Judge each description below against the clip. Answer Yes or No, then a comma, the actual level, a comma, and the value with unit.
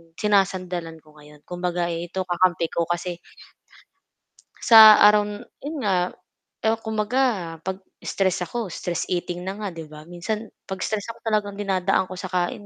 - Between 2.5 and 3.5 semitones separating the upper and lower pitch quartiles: Yes, average, 3.1 semitones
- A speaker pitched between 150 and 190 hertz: Yes, medium, 185 Hz